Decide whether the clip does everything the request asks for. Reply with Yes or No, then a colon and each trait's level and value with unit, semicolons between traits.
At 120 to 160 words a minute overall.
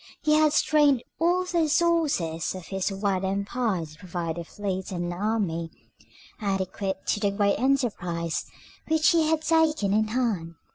Yes: average, 150 wpm